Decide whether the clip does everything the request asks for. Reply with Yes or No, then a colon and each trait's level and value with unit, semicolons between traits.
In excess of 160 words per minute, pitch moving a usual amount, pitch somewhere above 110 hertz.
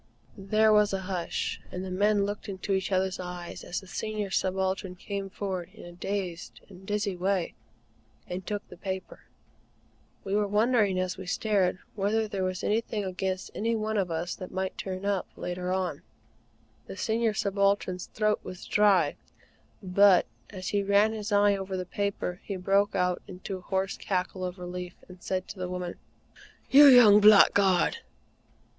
No: average, 170 wpm; narrow, 2.0 semitones; high, 190 Hz